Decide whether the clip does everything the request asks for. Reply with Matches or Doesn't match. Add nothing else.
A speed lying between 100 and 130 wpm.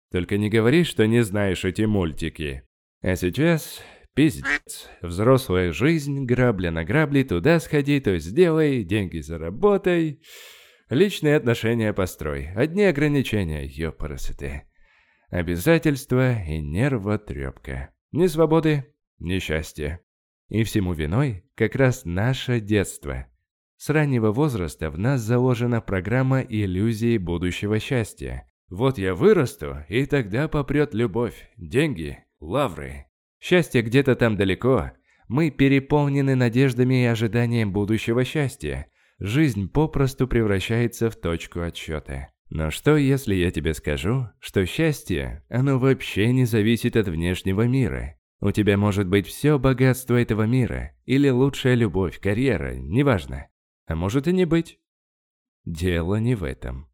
Matches